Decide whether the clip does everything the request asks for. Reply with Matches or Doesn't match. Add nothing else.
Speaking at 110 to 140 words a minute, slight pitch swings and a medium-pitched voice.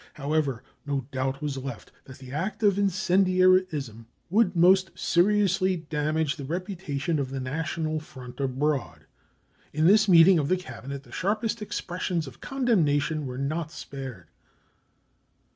Doesn't match